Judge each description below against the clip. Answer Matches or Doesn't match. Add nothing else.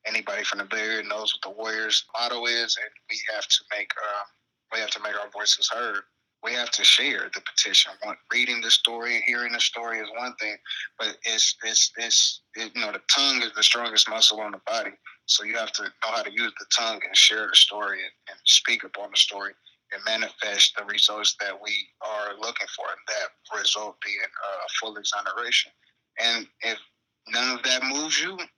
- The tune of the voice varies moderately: Doesn't match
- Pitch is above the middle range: Doesn't match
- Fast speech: Matches